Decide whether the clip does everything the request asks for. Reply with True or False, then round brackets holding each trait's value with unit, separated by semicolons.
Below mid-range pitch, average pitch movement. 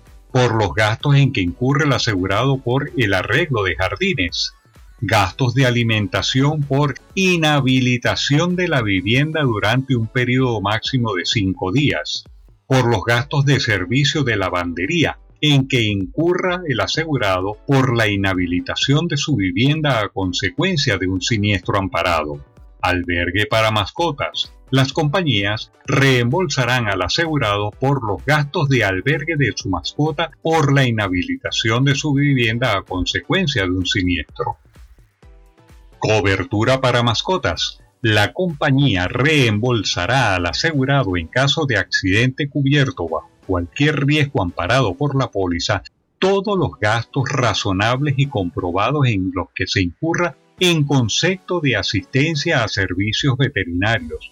False (125 Hz; 6.1 semitones)